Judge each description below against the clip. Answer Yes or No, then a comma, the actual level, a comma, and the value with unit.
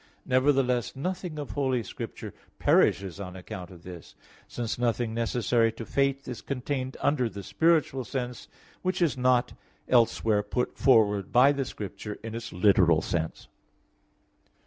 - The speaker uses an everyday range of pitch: Yes, average, 4.6 semitones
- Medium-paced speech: Yes, average, 145 wpm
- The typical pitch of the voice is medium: No, low, 120 Hz